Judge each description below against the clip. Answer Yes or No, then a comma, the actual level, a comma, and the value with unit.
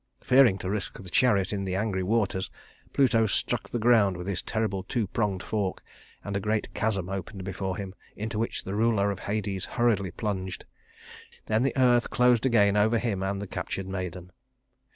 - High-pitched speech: No, low, 100 Hz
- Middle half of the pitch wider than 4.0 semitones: No, average, 2.8 semitones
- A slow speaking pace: No, average, 180 wpm